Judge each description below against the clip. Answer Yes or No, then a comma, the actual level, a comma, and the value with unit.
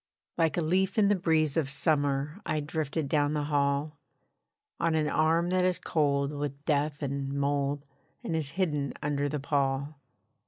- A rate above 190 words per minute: No, average, 165 wpm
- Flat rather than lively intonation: Yes, narrow, 2.3 semitones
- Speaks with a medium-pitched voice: Yes, medium, 150 Hz